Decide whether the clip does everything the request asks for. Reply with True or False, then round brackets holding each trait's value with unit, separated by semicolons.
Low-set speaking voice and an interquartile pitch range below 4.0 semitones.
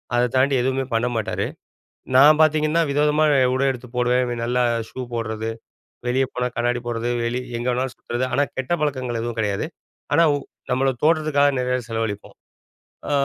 True (125 Hz; 2.8 semitones)